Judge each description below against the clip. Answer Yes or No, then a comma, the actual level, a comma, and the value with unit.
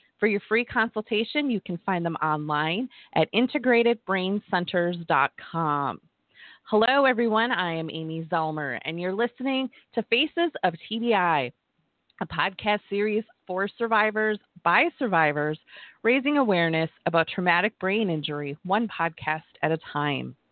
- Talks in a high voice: Yes, high, 195 Hz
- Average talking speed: No, slow, 125 wpm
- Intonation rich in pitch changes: Yes, wide, 6.0 semitones